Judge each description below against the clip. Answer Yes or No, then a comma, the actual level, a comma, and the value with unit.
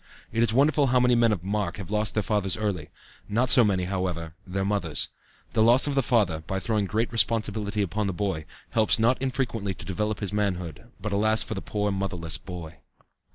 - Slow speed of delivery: No, average, 200 wpm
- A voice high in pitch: No, low, 105 Hz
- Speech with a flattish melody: No, average, 3.3 semitones